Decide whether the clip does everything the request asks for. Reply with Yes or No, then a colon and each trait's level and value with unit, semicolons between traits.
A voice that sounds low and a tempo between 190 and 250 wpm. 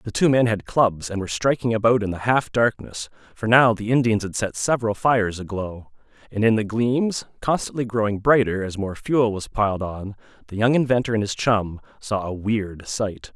Yes: low, 110 Hz; average, 200 wpm